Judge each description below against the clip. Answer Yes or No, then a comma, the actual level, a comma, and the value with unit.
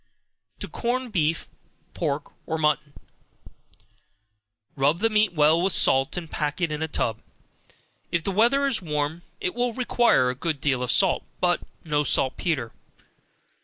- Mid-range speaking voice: Yes, medium, 160 Hz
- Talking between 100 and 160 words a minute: Yes, average, 150 wpm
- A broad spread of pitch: Yes, wide, 5.9 semitones